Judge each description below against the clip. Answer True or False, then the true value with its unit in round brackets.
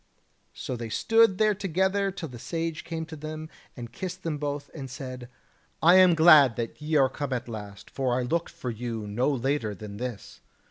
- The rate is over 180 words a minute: True (200 wpm)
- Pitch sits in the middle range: True (145 Hz)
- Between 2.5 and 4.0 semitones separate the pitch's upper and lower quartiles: False (5.4 semitones)